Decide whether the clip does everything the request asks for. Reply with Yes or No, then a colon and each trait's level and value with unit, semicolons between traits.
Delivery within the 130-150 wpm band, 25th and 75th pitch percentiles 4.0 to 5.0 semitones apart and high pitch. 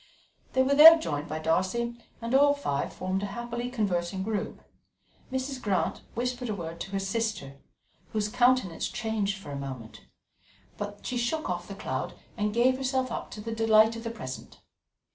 No: average, 175 wpm; average, 4.6 semitones; high, 220 Hz